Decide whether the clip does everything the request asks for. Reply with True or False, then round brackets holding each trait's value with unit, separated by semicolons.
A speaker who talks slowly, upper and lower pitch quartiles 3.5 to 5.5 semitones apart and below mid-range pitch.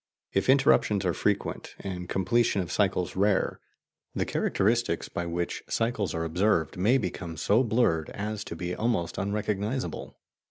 False (145 wpm; 3.8 semitones; 100 Hz)